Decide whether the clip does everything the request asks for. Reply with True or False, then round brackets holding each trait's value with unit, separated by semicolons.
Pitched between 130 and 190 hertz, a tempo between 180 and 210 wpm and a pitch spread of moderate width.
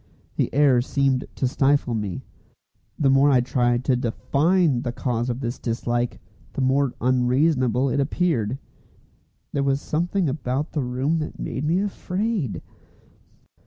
False (135 Hz; 140 wpm; 3.1 semitones)